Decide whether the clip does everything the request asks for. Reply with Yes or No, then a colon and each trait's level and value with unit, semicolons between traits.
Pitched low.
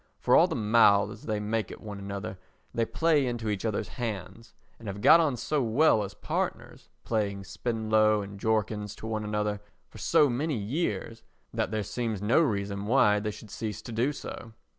Yes: low, 110 Hz